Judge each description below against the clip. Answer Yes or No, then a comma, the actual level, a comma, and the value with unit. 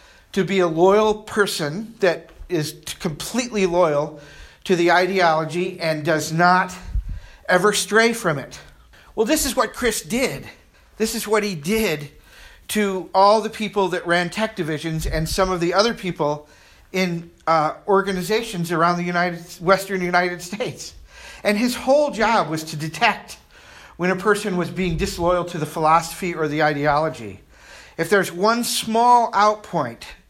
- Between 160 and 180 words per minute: No, average, 150 wpm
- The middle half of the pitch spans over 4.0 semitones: Yes, average, 4.6 semitones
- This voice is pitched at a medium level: Yes, medium, 180 Hz